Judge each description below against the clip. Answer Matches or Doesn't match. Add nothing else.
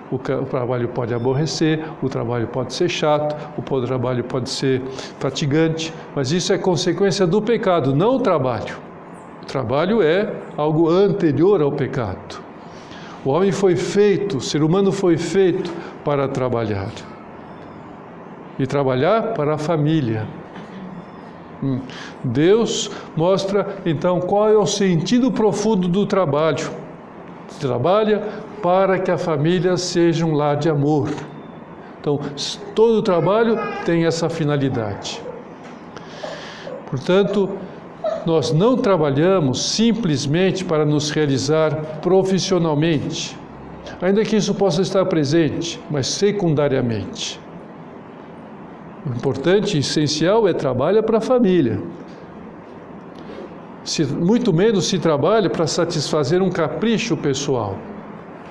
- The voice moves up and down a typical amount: Matches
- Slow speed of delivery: Matches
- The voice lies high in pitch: Doesn't match